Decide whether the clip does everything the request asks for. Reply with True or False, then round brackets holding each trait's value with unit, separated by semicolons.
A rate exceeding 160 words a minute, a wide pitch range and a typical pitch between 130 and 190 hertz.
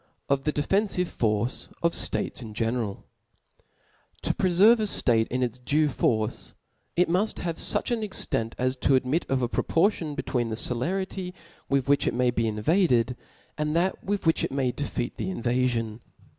True (180 wpm; 6.5 semitones; 135 Hz)